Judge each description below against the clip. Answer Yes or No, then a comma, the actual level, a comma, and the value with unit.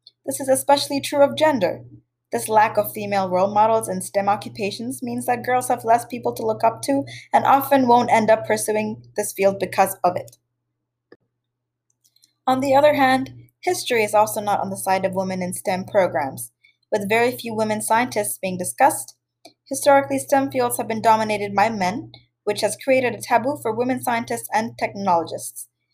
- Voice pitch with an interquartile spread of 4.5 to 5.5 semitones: Yes, average, 4.9 semitones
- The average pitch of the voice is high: Yes, high, 215 Hz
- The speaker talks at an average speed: Yes, average, 180 wpm